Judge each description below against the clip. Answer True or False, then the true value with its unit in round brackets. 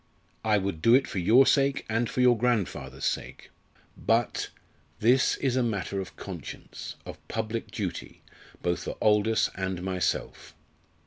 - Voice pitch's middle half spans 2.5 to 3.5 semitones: False (4.1 semitones)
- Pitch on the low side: True (110 Hz)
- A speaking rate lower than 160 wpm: True (145 wpm)